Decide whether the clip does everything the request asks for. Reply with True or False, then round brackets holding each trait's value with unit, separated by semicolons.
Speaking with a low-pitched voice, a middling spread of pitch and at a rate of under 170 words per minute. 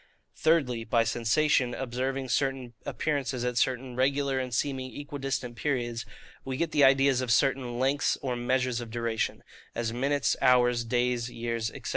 False (125 Hz; 2.1 semitones; 150 wpm)